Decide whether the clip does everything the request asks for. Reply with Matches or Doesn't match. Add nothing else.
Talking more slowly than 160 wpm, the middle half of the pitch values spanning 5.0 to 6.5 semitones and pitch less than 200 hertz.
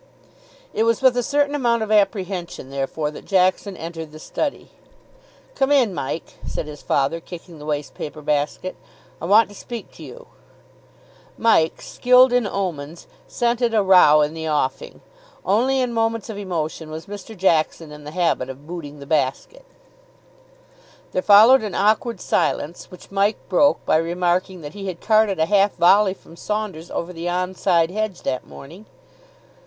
Doesn't match